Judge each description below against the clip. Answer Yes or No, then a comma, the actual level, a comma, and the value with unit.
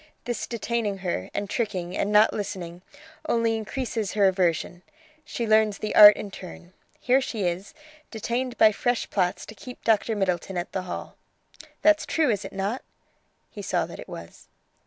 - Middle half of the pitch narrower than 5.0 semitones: Yes, average, 3.7 semitones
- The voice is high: Yes, high, 210 Hz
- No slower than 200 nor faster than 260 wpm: No, average, 170 wpm